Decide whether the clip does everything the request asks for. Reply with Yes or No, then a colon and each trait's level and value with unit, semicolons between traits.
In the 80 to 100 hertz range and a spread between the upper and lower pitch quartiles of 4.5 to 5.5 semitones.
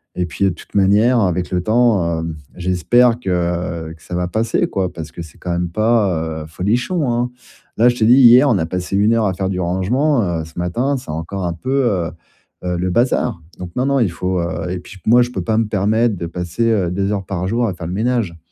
Yes: very low, 95 Hz; average, 5.0 semitones